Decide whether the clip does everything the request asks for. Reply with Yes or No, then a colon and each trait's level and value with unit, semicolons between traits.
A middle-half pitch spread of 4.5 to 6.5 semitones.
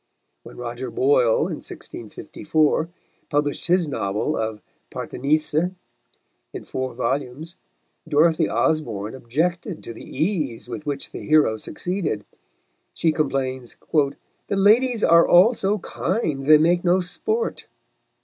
Yes: average, 5.0 semitones